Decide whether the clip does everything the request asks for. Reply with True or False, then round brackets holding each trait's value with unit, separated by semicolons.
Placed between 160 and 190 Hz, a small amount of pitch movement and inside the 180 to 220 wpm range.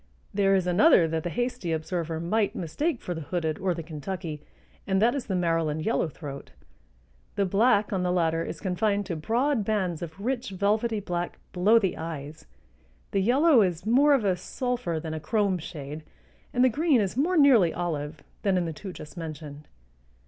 False (185 Hz; 5.2 semitones; 185 wpm)